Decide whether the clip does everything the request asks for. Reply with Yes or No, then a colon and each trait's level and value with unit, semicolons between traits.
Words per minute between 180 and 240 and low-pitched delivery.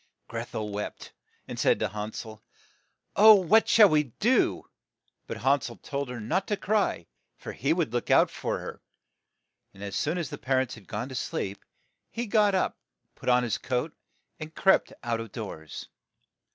Yes: average, 185 wpm; low, 130 Hz